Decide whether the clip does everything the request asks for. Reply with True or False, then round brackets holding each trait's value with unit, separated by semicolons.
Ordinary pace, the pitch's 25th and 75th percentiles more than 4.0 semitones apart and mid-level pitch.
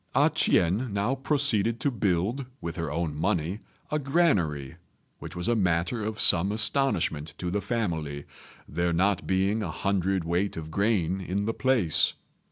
False (155 wpm; 5.0 semitones; 95 Hz)